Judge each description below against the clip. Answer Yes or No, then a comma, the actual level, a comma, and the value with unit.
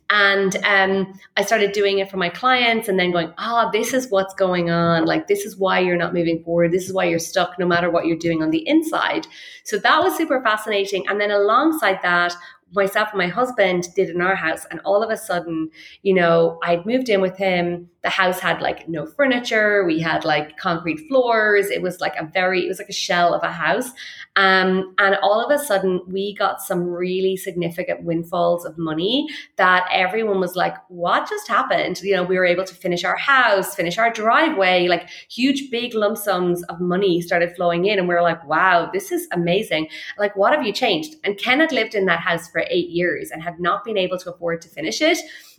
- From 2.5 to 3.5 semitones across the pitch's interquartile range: Yes, average, 3.0 semitones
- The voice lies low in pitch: No, high, 190 Hz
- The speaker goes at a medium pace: No, fast, 220 wpm